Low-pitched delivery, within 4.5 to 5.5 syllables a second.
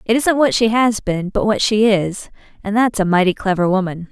No: high, 205 Hz; 5.2 syllables/s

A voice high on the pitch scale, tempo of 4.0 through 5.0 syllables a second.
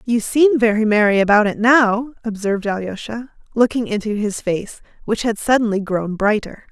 Yes: high, 220 Hz; 4.9 syllables/s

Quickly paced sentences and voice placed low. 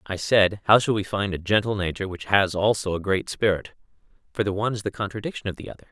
Yes: fast, 245 wpm; low, 100 Hz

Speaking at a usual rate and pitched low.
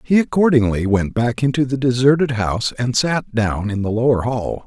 Yes: average, 195 wpm; low, 120 Hz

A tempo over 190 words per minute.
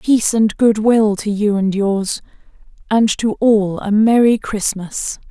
No: average, 160 wpm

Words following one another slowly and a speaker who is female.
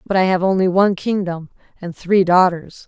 No: average, 190 wpm; female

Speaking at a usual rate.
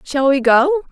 Yes: average, 195 wpm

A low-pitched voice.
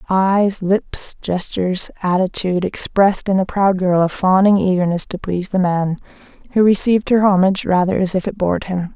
No: high, 190 Hz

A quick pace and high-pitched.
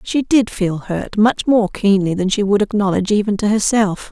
No: average, 190 wpm; high, 205 Hz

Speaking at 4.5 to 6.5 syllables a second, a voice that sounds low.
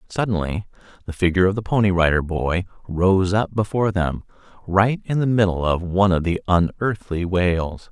Yes: 5.3 syllables/s; very low, 95 Hz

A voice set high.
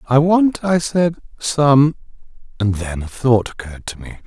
No: low, 135 Hz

